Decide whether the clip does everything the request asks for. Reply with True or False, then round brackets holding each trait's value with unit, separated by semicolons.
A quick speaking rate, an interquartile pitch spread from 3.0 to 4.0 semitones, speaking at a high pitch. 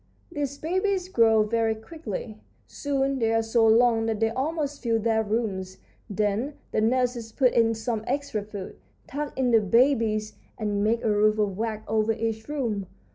False (170 wpm; 3.3 semitones; 225 Hz)